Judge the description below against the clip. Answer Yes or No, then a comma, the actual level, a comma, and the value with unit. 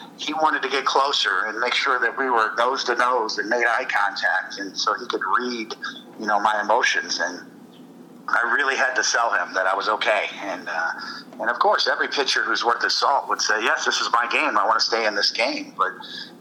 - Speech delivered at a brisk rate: Yes, fast, 235 wpm